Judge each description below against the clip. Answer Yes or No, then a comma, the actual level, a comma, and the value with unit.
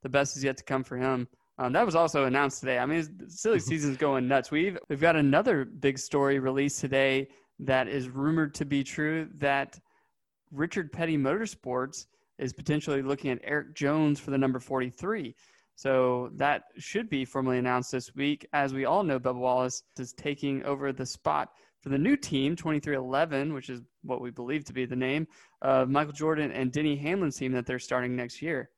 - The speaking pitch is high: No, medium, 140 Hz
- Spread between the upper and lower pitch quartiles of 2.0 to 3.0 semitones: Yes, narrow, 2.5 semitones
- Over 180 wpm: Yes, average, 195 wpm